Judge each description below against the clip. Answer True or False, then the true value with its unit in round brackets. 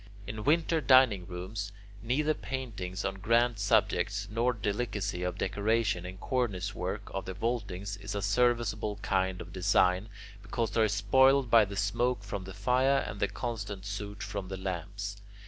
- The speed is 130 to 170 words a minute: True (165 wpm)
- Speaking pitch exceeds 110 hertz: False (105 Hz)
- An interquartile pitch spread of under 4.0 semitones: True (3.3 semitones)